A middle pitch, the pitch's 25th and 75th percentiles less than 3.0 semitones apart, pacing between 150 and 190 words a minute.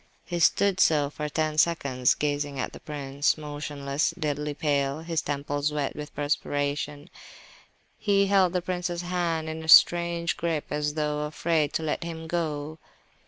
Yes: medium, 150 Hz; narrow, 2.6 semitones; average, 155 wpm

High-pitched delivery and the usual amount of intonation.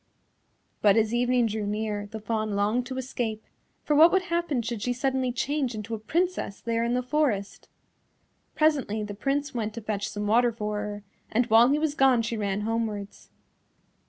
Yes: high, 230 Hz; average, 3.7 semitones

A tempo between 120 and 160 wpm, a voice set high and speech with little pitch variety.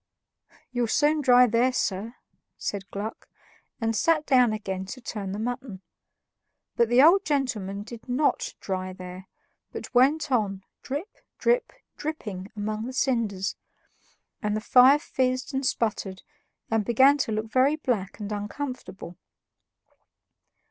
No: slow, 135 wpm; high, 235 Hz; average, 4.4 semitones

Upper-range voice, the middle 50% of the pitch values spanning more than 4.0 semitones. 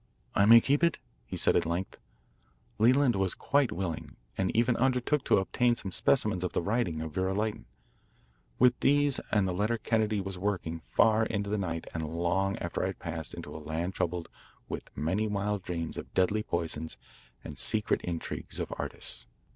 No: low, 100 Hz; average, 4.7 semitones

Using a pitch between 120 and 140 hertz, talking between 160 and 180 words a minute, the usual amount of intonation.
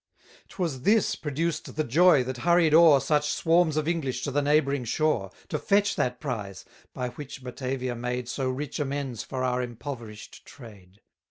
Yes: low, 135 Hz; average, 165 wpm; average, 3.8 semitones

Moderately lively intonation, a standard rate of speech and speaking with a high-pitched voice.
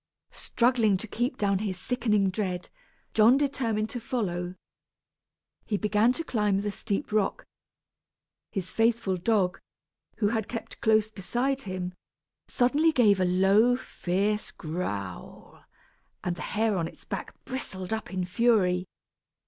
No: average, 3.9 semitones; slow, 130 wpm; high, 210 Hz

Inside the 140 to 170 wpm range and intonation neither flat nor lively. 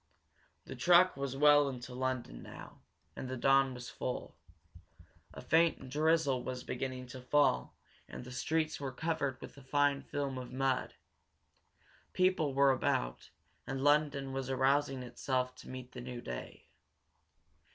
No: average, 145 wpm; narrow, 2.2 semitones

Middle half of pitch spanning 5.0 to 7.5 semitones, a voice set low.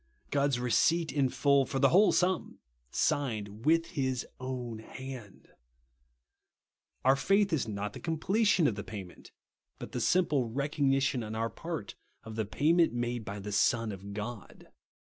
Yes: wide, 5.5 semitones; low, 130 Hz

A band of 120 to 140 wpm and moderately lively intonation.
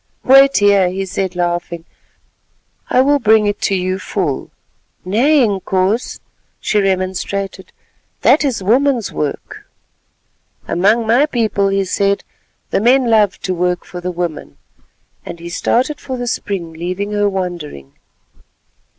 Yes: slow, 135 wpm; average, 4.1 semitones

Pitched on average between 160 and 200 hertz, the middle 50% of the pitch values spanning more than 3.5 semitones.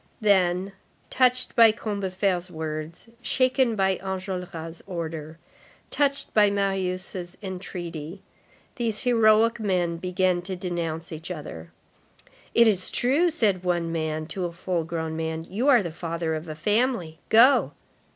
Yes: medium, 185 Hz; average, 4.3 semitones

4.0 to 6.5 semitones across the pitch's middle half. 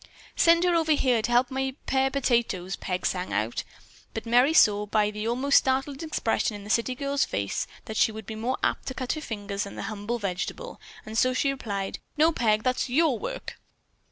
Yes: average, 4.6 semitones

